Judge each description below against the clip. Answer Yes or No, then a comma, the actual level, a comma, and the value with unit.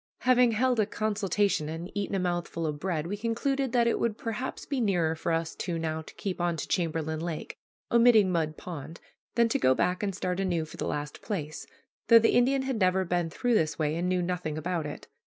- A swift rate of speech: Yes, fast, 220 wpm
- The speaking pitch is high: No, medium, 180 Hz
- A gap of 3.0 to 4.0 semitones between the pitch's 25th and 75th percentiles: No, wide, 5.4 semitones